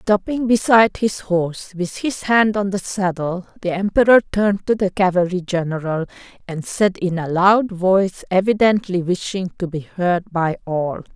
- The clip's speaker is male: No, female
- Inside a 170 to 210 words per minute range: No, average, 160 wpm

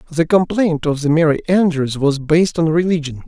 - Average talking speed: Yes, average, 185 wpm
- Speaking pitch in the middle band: Yes, medium, 160 Hz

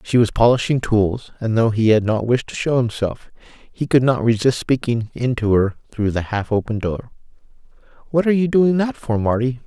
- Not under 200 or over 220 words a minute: Yes, fast, 205 wpm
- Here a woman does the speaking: No, male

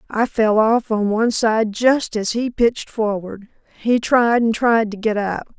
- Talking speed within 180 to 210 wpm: Yes, average, 195 wpm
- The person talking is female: Yes, female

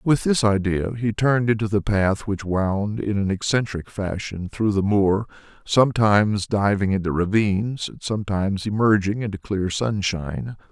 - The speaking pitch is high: No, low, 105 Hz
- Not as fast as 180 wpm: Yes, average, 150 wpm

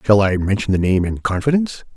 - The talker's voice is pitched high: No, low, 105 Hz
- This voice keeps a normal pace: No, fast, 215 wpm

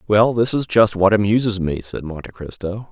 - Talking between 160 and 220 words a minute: Yes, fast, 205 wpm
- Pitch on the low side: Yes, low, 100 Hz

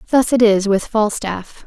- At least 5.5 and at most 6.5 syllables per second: No, 4.2 syllables/s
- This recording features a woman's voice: Yes, female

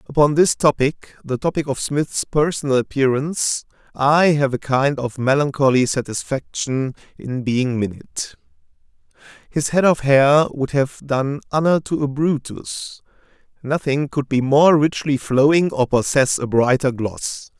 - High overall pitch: No, low, 135 Hz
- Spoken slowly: Yes, slow, 130 wpm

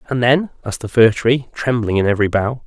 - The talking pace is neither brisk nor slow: No, fast, 225 wpm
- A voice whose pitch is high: No, low, 120 Hz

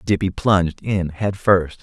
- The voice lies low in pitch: Yes, very low, 95 Hz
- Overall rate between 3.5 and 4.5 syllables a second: Yes, 4.1 syllables/s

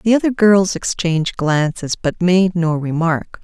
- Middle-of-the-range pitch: Yes, medium, 175 Hz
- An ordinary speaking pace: Yes, average, 155 wpm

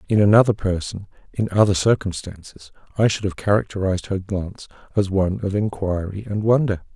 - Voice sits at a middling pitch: No, low, 100 Hz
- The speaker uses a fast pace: No, average, 155 wpm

